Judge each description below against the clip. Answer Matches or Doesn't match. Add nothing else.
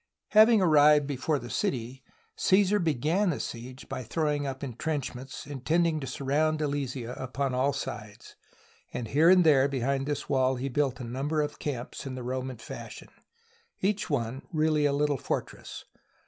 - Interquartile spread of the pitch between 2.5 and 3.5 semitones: Matches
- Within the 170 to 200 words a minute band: Doesn't match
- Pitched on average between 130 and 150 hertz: Matches